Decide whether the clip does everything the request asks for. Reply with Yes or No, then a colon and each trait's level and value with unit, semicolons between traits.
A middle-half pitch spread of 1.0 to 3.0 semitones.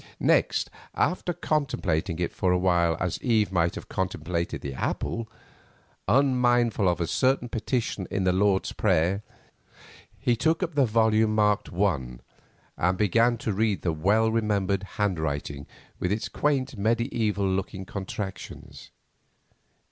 No: average, 4.3 semitones